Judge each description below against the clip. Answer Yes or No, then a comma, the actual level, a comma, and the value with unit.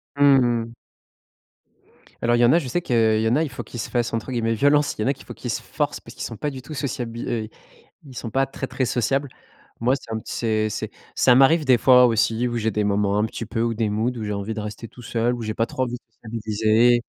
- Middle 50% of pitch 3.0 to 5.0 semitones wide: No, narrow, 2.6 semitones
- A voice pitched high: No, low, 120 Hz